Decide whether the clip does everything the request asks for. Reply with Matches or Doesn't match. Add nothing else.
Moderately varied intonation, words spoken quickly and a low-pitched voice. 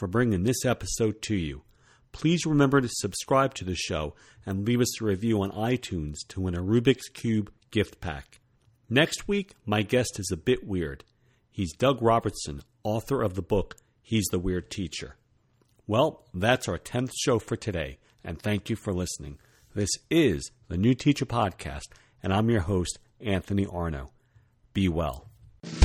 Doesn't match